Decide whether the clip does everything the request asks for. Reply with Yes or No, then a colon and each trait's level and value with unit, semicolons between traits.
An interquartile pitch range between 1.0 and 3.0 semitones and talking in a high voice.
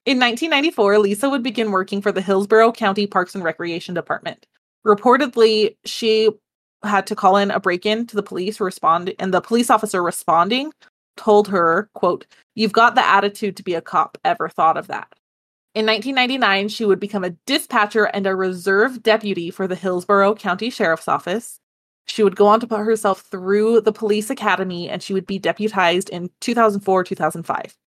Yes: average, 2.7 semitones; high, 205 Hz